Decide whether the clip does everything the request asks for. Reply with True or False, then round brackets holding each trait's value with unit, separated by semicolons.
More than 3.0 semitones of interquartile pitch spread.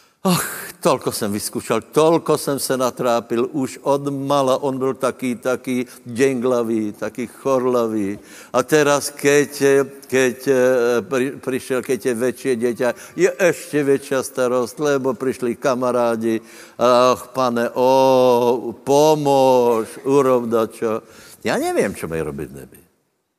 False (2.4 semitones)